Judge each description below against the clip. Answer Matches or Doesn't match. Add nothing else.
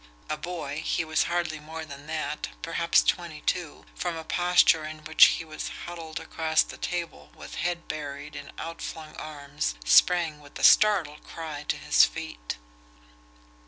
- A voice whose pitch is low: Doesn't match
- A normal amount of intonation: Doesn't match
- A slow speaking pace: Doesn't match